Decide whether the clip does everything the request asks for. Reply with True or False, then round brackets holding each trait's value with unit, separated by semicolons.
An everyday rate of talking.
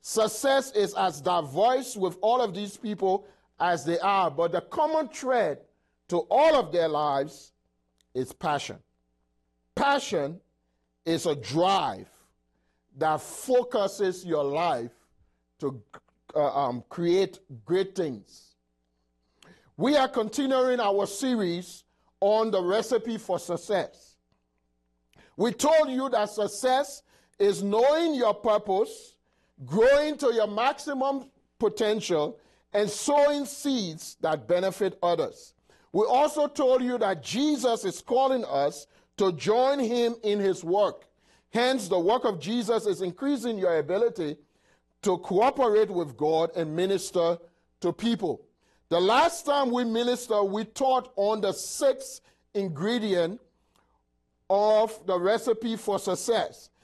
False (120 wpm)